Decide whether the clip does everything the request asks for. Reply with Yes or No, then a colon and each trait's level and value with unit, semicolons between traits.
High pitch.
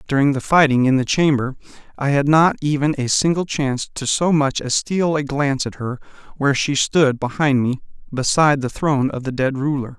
No: medium, 140 Hz